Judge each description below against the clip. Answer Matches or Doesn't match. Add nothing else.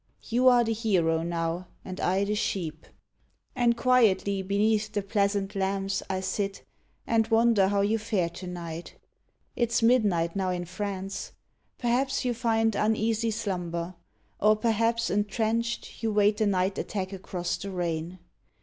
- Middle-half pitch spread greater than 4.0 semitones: Doesn't match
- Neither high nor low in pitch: Doesn't match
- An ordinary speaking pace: Matches